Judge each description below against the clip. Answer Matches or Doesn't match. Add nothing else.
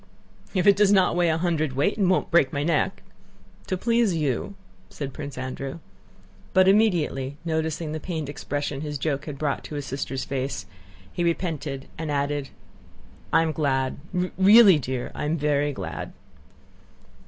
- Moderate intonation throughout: Matches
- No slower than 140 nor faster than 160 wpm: Matches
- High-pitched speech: Doesn't match